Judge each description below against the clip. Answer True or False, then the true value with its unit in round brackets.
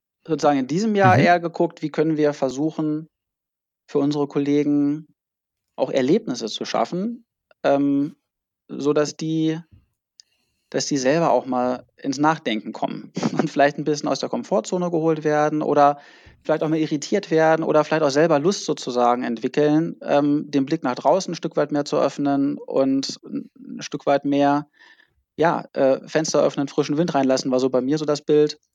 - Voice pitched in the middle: True (150 Hz)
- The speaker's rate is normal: True (165 wpm)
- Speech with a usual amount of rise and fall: False (2.0 semitones)